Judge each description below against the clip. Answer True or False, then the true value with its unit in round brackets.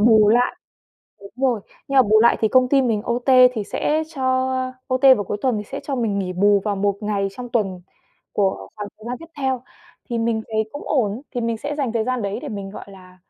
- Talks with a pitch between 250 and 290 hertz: False (225 Hz)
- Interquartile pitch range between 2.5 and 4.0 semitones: True (3.7 semitones)